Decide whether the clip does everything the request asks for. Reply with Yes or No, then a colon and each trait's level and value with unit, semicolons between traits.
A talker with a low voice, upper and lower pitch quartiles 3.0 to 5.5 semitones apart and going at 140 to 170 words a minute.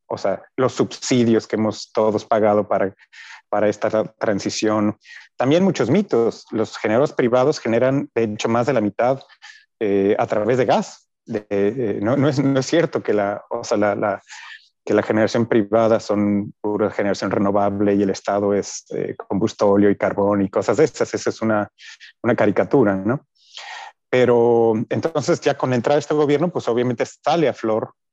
No: low, 110 Hz; average, 3.6 semitones; average, 180 wpm